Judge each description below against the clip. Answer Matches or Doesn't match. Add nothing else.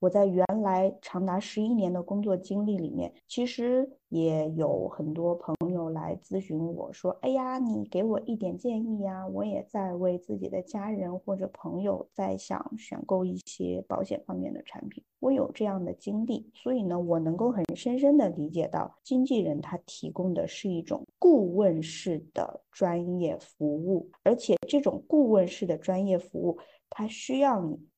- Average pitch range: Matches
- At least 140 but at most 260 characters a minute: Matches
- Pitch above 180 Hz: Matches